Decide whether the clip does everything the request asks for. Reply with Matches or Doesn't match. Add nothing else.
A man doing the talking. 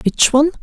Doesn't match